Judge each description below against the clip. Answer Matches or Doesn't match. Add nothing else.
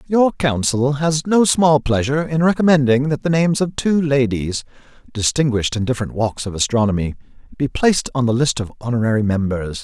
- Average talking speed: Matches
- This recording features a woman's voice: Doesn't match